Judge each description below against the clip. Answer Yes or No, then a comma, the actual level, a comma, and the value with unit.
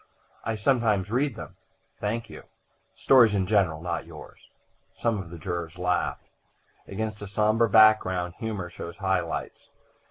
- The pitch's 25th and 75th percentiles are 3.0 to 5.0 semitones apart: Yes, average, 3.6 semitones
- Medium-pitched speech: No, low, 105 Hz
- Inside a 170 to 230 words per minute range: No, average, 145 wpm